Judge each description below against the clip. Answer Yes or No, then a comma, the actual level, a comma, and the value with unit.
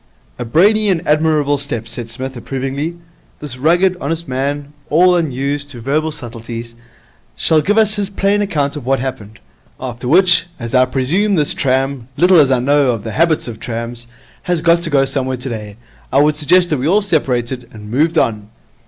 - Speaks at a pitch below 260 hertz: Yes, medium, 140 Hz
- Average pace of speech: Yes, average, 185 wpm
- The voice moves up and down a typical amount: Yes, average, 5.0 semitones